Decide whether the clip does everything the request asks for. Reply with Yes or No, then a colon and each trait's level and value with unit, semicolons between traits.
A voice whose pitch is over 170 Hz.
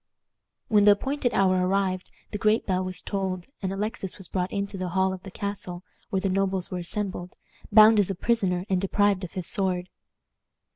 Yes: high, 190 Hz